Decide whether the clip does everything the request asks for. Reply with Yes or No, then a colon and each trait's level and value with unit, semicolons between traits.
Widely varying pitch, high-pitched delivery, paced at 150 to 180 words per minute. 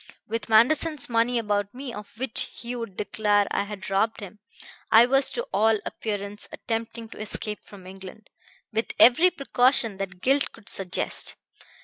No: average, 3.1 semitones; high, 220 Hz; average, 155 wpm